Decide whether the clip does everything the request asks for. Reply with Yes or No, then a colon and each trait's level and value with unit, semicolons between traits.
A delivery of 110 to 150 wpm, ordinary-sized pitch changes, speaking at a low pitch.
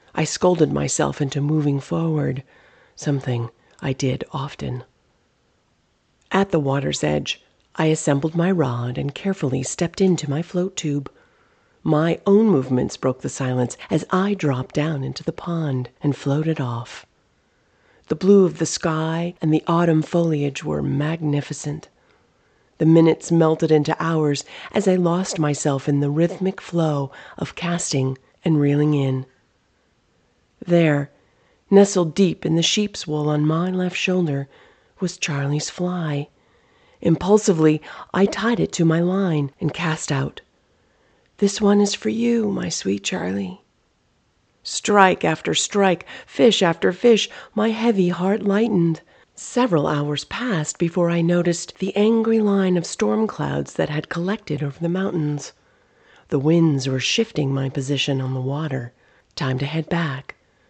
No: average, 140 wpm; average, 4.3 semitones; medium, 160 Hz